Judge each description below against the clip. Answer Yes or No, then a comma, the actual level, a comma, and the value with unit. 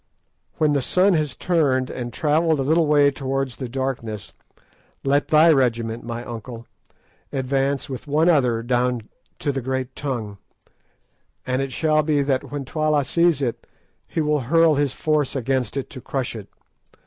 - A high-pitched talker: No, low, 135 Hz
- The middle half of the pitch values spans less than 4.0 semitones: Yes, average, 3.3 semitones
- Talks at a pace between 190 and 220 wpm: No, average, 160 wpm